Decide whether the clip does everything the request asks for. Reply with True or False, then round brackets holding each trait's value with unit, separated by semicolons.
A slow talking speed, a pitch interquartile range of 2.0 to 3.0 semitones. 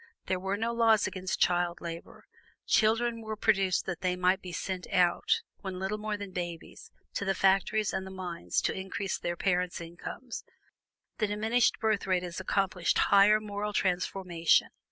False (165 wpm; 2.6 semitones)